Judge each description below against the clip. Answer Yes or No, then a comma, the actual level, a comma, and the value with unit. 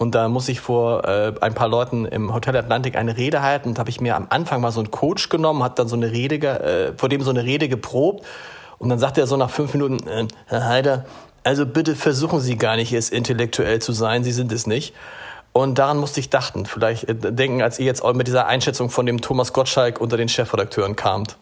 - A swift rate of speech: Yes, fast, 240 wpm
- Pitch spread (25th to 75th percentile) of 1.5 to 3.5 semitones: Yes, average, 2.7 semitones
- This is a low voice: Yes, low, 125 Hz